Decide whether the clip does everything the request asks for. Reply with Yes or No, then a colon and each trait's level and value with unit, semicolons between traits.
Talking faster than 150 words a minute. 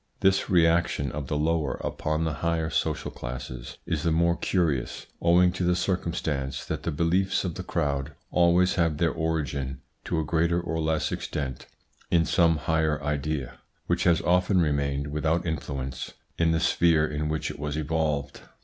Yes: average, 165 wpm